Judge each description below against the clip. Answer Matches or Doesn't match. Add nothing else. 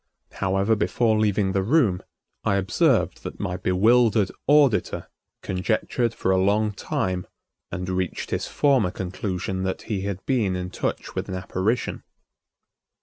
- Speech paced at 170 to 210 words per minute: Doesn't match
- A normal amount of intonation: Matches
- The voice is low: Matches